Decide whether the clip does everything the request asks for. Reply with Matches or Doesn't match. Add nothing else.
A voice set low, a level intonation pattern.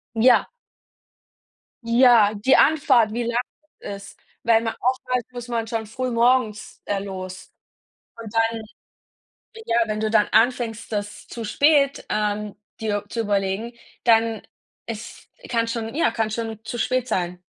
Doesn't match